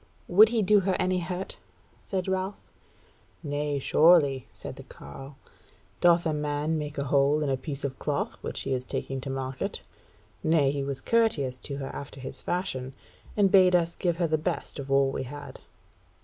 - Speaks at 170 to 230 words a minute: Yes, average, 185 wpm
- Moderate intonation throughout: Yes, average, 4.6 semitones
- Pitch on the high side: No, medium, 145 Hz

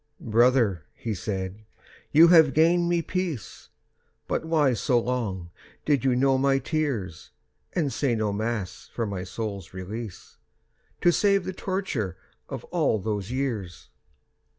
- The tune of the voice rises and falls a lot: Yes, wide, 7.2 semitones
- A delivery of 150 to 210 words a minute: No, slow, 135 wpm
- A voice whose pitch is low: Yes, low, 120 Hz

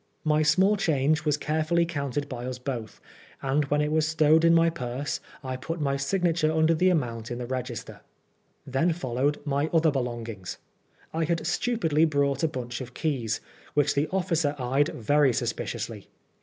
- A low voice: No, medium, 145 Hz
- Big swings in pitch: No, average, 3.9 semitones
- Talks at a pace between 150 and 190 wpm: Yes, average, 170 wpm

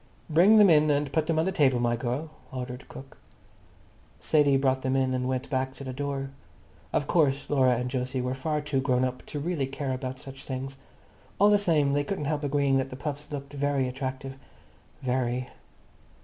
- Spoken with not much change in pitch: Yes, narrow, 2.2 semitones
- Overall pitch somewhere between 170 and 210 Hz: No, low, 135 Hz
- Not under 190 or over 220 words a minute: Yes, average, 195 wpm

